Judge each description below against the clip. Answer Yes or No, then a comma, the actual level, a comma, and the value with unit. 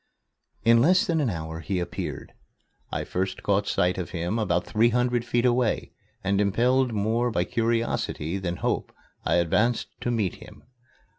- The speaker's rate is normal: Yes, average, 160 wpm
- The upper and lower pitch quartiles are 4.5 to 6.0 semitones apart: Yes, average, 4.8 semitones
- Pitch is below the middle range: Yes, low, 110 Hz